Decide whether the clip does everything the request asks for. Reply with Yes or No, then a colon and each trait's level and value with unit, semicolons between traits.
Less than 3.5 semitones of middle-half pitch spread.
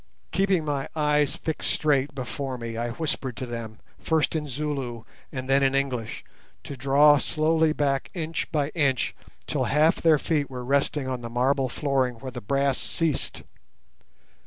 Yes: average, 2.8 semitones